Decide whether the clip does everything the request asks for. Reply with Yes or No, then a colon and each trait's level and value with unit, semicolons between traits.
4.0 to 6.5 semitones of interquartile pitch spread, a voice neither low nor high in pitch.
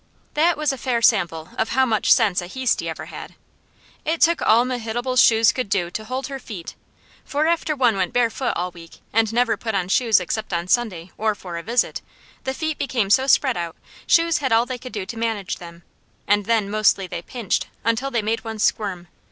No: average, 4.7 semitones; high, 225 Hz